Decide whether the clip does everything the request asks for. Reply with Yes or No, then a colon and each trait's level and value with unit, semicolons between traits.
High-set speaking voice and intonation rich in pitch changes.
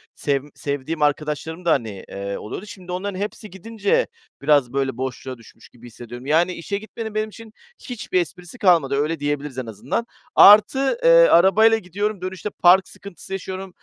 No: medium, 175 Hz; wide, 6.5 semitones